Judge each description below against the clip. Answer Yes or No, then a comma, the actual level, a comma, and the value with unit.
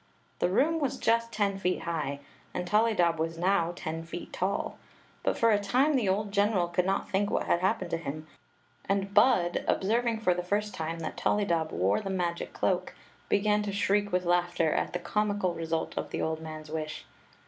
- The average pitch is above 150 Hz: Yes, medium, 185 Hz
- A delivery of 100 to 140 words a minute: No, average, 190 wpm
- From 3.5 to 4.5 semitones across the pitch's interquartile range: Yes, average, 3.8 semitones